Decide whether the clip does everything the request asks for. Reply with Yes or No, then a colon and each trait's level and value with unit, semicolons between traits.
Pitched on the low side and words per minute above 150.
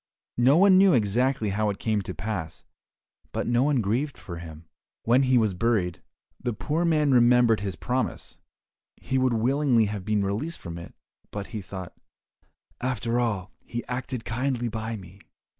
Yes: low, 115 Hz; average, 165 wpm